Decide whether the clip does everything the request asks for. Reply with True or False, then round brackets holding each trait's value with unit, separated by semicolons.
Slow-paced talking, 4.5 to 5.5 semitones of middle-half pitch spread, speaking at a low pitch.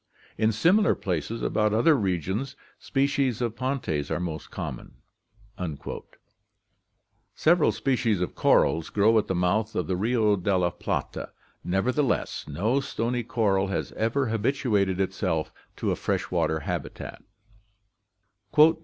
True (120 wpm; 5.1 semitones; 110 Hz)